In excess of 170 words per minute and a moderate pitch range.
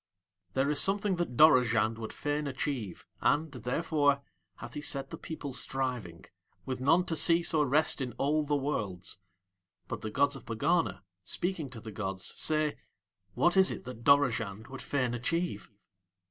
No: average, 160 wpm; average, 4.7 semitones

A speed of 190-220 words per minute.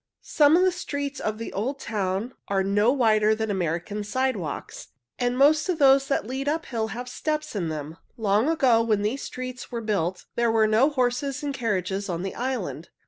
Yes: average, 195 wpm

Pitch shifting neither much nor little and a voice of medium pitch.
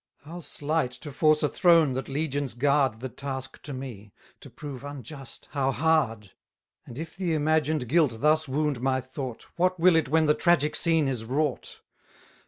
Yes: average, 3.2 semitones; medium, 145 Hz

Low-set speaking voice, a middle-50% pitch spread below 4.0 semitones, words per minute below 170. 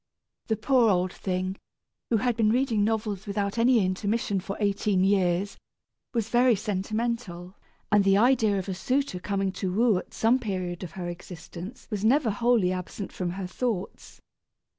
No: high, 200 Hz; average, 3.6 semitones; average, 160 wpm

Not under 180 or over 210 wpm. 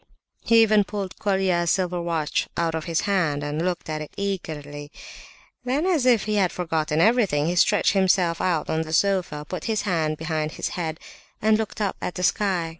Yes: average, 190 wpm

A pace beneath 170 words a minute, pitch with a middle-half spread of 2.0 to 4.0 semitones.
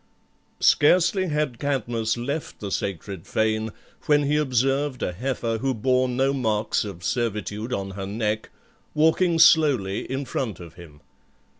No: average, 140 wpm; average, 5.2 semitones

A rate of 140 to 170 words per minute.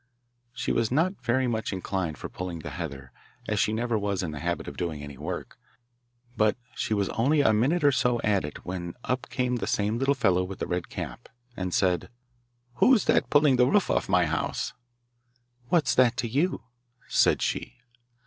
No: average, 190 wpm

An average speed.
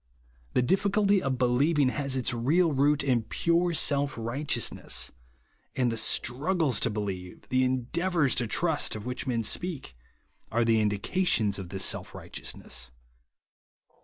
Yes: average, 150 wpm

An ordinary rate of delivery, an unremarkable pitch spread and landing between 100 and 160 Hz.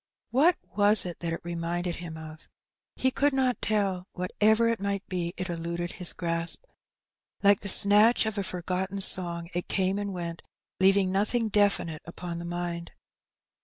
No: average, 165 wpm; average, 3.1 semitones; medium, 185 Hz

